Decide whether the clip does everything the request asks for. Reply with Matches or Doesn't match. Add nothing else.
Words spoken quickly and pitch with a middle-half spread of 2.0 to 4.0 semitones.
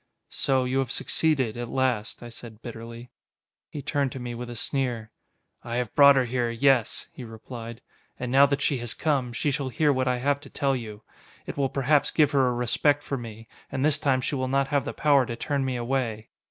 Matches